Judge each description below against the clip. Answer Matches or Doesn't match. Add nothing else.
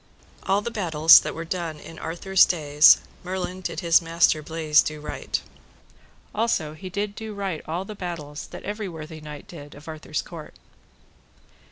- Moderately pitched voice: Matches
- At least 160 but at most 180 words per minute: Matches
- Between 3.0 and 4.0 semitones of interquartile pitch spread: Matches